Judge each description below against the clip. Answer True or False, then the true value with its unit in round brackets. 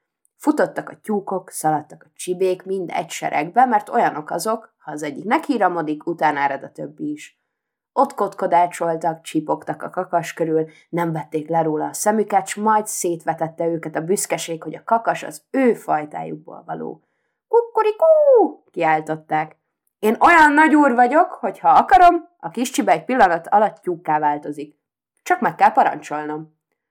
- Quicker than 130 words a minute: True (150 wpm)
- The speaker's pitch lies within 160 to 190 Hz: True (185 Hz)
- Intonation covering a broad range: True (8.4 semitones)